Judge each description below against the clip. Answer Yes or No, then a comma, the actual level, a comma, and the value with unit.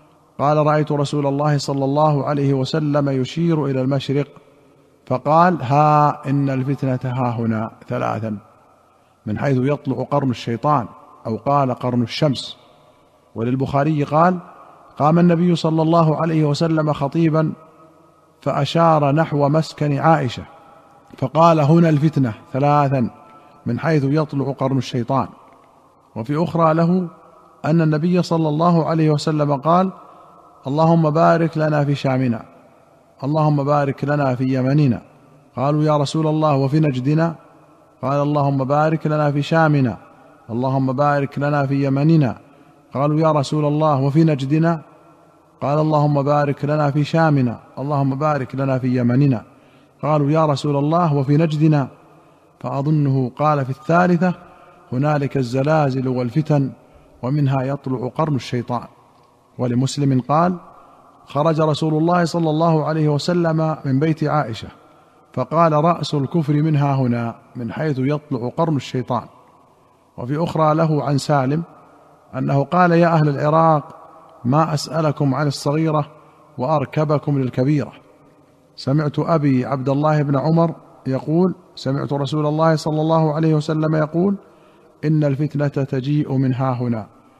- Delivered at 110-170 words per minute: Yes, average, 120 wpm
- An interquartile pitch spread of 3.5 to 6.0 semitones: No, average, 2.7 semitones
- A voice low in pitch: No, medium, 145 Hz